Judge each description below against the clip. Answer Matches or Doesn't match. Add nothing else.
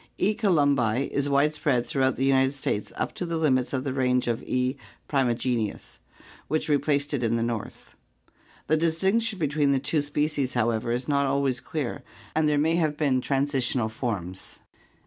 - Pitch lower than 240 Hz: Matches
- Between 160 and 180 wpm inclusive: Matches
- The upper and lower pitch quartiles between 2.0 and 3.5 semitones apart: Matches